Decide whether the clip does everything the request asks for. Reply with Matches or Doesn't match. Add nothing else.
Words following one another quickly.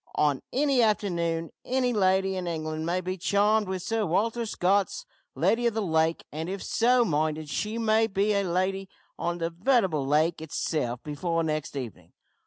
Doesn't match